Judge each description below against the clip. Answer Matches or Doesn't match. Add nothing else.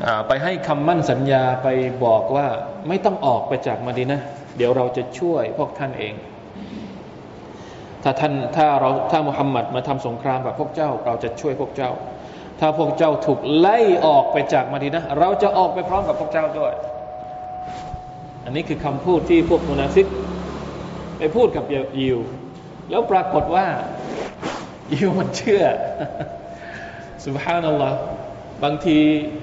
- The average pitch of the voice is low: Doesn't match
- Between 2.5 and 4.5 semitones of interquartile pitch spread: Matches